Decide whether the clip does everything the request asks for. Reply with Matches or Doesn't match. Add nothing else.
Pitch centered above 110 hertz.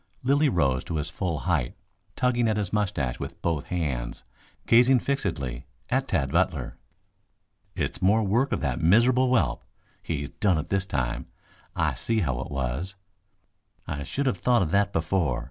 Doesn't match